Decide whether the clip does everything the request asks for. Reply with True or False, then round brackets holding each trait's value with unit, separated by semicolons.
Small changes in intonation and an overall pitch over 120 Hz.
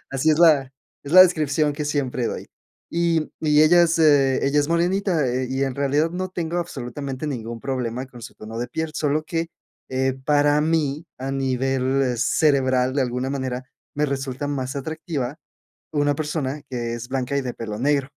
False (3.0 semitones; 140 Hz)